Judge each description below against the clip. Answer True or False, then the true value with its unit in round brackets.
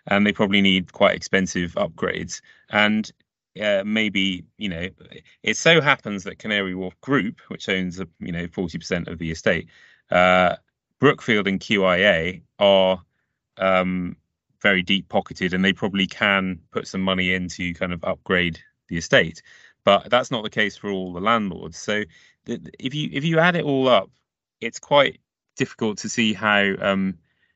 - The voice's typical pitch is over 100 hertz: False (95 Hz)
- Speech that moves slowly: False (170 wpm)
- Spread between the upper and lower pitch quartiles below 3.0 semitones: True (2.5 semitones)